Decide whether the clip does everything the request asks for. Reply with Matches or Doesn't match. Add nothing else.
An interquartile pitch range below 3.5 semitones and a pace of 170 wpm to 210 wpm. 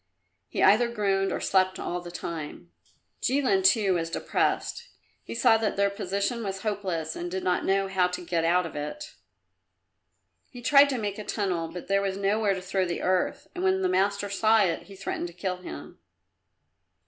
Matches